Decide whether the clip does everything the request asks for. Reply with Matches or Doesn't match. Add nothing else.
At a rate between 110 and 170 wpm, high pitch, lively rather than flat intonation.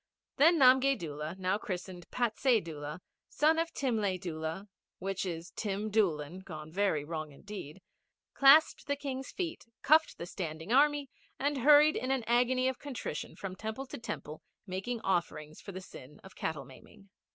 Matches